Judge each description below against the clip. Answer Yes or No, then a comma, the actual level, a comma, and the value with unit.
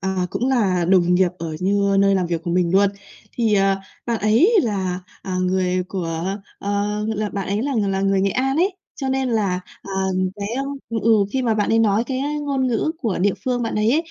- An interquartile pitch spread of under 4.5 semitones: Yes, average, 3.8 semitones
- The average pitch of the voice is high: Yes, high, 200 Hz